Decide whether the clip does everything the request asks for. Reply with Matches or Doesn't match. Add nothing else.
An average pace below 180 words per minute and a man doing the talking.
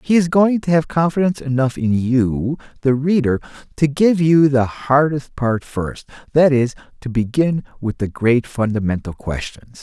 Matches